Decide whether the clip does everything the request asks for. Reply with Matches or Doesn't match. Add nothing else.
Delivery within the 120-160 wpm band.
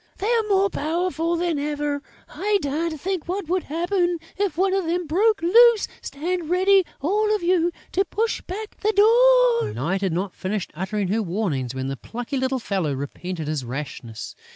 Doesn't match